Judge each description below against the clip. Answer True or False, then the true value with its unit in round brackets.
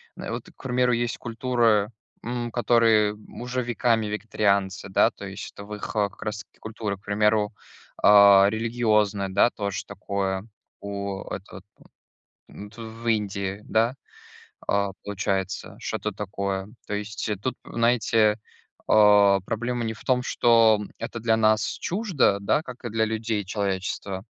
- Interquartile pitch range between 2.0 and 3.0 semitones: True (2.5 semitones)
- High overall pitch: False (105 Hz)